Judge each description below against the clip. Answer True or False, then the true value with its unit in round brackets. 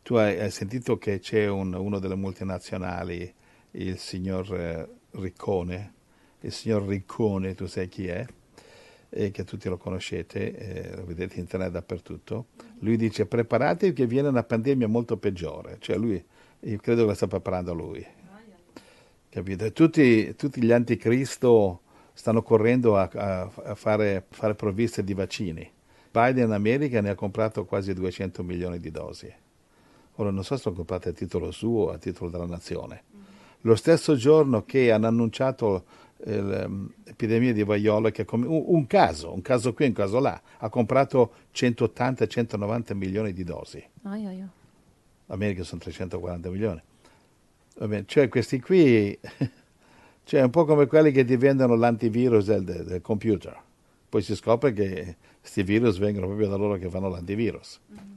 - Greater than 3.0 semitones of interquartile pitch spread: True (4.2 semitones)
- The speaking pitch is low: True (105 Hz)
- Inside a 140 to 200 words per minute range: True (150 wpm)